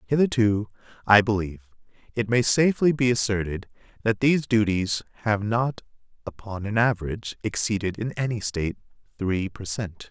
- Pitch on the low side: Yes, low, 110 Hz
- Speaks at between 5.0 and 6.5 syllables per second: Yes, 5.4 syllables/s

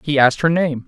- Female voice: No, male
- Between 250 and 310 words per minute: Yes, fast, 275 wpm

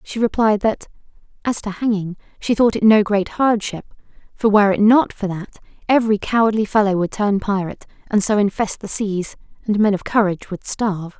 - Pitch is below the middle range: No, high, 205 Hz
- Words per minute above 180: Yes, average, 190 wpm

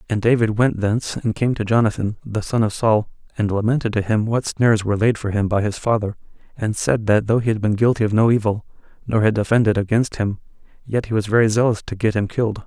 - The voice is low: Yes, low, 110 Hz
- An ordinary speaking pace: No, fast, 235 wpm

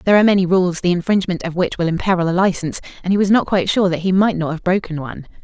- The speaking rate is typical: No, fast, 275 wpm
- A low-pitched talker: No, medium, 180 Hz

